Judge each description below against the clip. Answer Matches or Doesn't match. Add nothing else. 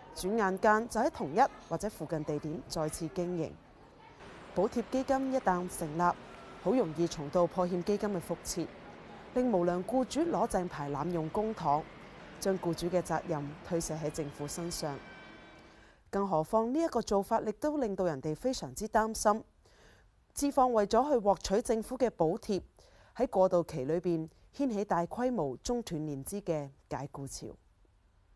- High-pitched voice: Doesn't match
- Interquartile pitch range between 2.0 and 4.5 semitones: Doesn't match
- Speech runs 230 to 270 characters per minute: Matches